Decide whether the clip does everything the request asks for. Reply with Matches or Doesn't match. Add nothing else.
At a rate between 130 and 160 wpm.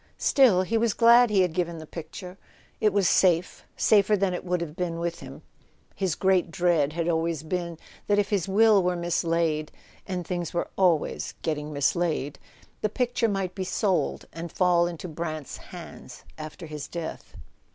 Doesn't match